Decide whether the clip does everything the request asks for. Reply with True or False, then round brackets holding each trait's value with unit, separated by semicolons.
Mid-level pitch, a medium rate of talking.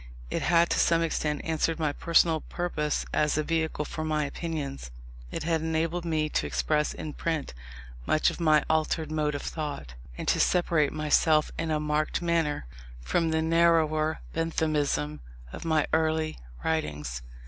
True (155 Hz; 160 wpm)